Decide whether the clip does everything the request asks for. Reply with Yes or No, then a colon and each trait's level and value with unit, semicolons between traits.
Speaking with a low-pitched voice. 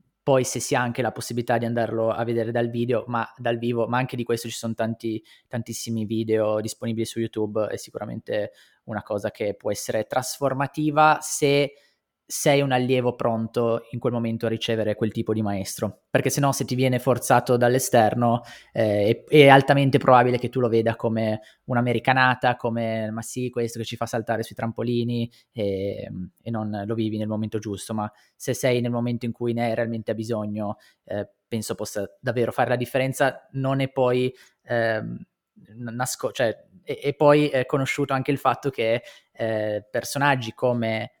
Yes: low, 120 Hz